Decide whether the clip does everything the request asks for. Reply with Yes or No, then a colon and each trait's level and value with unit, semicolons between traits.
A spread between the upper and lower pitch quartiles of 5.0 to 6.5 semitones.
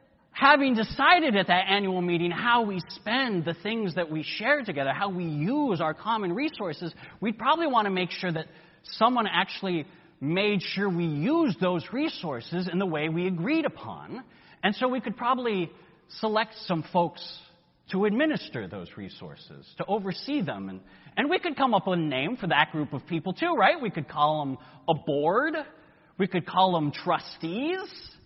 Yes: wide, 5.6 semitones